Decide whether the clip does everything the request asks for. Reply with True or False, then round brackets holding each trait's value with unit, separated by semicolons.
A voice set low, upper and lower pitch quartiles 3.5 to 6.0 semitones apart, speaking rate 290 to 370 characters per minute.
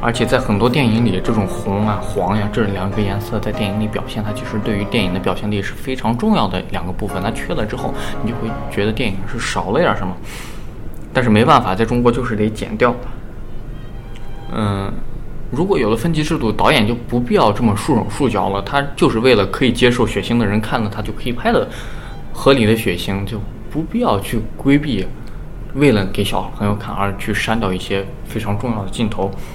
False (110 Hz; 3.0 semitones; 310 characters per minute)